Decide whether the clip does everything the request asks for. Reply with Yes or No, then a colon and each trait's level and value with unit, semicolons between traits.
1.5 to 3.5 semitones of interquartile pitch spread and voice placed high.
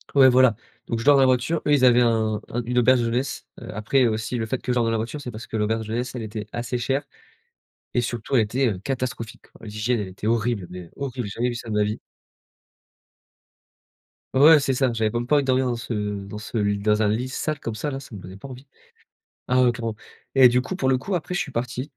No: average, 3.0 semitones; low, 120 Hz